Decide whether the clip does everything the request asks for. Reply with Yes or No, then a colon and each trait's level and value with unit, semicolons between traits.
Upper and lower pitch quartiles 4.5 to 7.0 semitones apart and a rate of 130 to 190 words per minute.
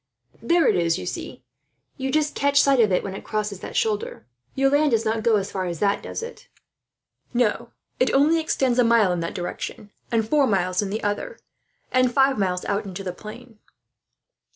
No: average, 5.3 semitones; average, 200 wpm